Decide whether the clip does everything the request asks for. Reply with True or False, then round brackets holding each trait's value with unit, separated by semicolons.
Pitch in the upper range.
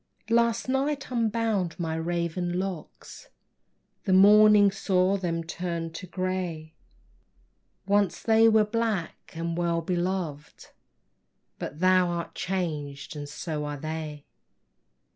False (180 Hz)